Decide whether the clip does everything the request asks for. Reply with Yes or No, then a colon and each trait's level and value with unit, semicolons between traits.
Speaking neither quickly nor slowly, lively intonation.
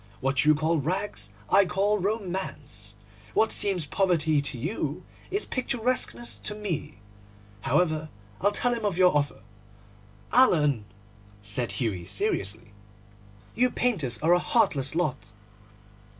No: slow, 120 wpm; wide, 8.6 semitones